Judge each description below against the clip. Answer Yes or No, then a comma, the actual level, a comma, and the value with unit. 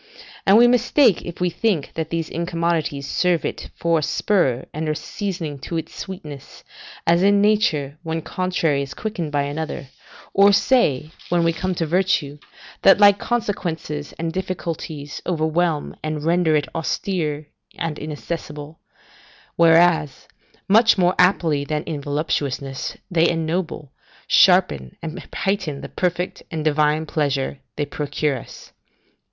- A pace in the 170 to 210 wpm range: No, average, 140 wpm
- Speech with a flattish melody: No, average, 3.4 semitones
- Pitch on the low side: No, medium, 160 Hz